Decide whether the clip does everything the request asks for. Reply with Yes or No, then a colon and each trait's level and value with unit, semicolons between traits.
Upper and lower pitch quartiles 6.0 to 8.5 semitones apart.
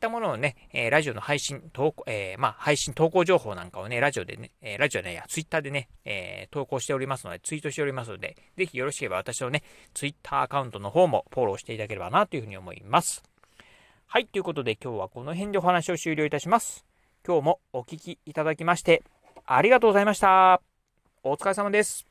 No: wide, 5.6 semitones